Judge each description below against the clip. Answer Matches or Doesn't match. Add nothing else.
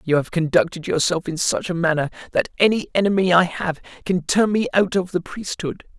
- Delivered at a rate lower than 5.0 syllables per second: Doesn't match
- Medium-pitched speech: Matches